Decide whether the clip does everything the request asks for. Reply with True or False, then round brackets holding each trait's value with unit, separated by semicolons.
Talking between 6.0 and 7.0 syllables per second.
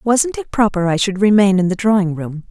False (5.3 syllables/s)